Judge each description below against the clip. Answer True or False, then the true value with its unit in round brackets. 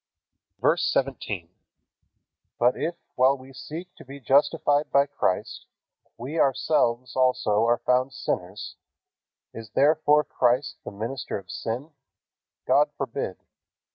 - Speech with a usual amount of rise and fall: True (3.6 semitones)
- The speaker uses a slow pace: True (115 wpm)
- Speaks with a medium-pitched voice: False (130 Hz)